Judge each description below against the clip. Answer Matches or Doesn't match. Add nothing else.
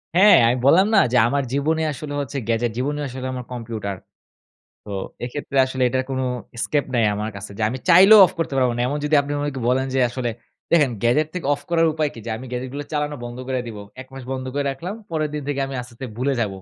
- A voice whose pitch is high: Doesn't match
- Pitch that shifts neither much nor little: Matches